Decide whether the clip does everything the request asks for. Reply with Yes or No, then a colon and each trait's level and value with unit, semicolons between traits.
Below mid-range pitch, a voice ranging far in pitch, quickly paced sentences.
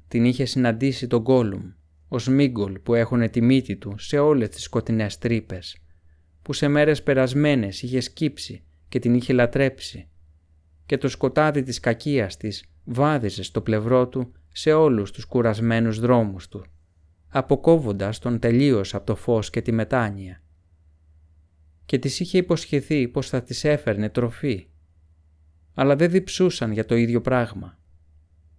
No: low, 115 Hz; wide, 7.2 semitones; average, 145 wpm